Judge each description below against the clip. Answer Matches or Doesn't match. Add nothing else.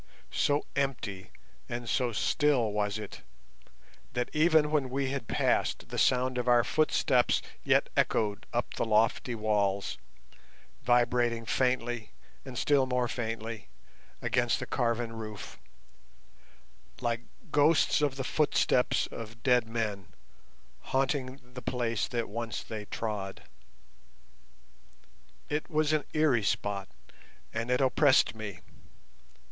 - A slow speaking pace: Matches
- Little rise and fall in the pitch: Doesn't match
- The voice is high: Doesn't match